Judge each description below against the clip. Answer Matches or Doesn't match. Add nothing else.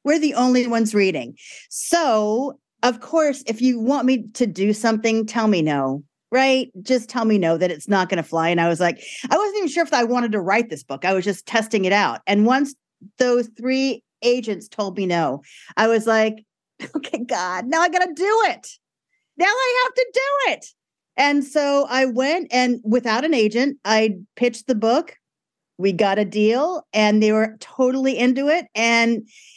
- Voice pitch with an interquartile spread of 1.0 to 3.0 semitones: Doesn't match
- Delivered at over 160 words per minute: Matches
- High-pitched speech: Matches